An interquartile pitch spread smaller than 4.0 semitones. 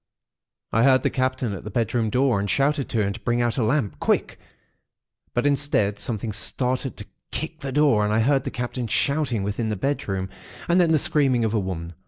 No: average, 4.6 semitones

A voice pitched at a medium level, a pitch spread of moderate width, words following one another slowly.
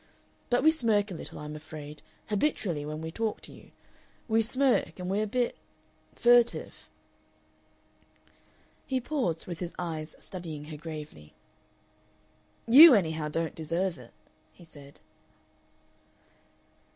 No: medium, 175 Hz; wide, 6.6 semitones; slow, 125 wpm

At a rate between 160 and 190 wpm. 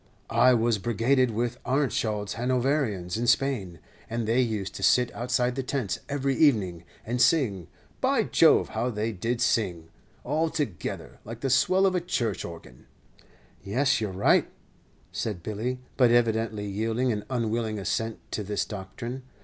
No: average, 150 wpm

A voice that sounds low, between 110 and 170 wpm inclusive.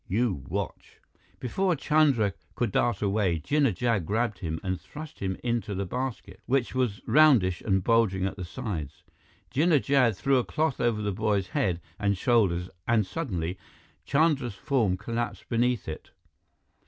Yes: low, 110 Hz; average, 155 wpm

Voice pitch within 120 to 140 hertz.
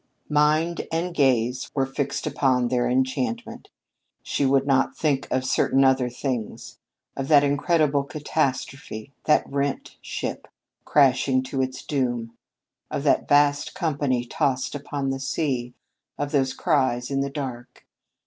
Yes: low, 135 Hz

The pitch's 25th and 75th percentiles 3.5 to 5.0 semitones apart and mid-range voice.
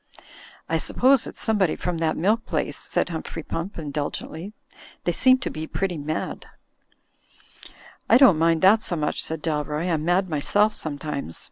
Yes: average, 4.4 semitones; medium, 165 Hz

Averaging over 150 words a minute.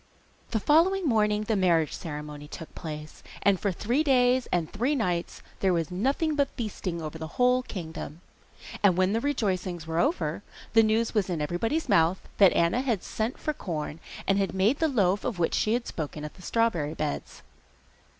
Yes: average, 185 wpm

